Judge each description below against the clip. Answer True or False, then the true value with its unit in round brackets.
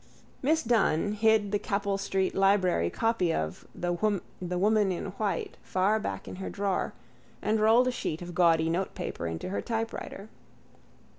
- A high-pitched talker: True (195 Hz)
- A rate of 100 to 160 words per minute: True (150 wpm)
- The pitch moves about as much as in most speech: True (3.4 semitones)